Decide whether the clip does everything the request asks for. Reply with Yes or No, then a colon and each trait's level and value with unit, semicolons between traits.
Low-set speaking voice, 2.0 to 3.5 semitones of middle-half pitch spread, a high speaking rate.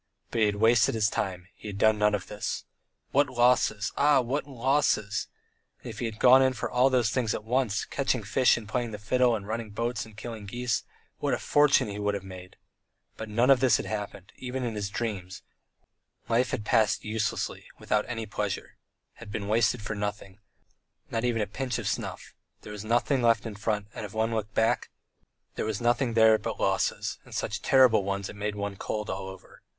Yes: low, 110 Hz; average, 2.9 semitones; fast, 210 wpm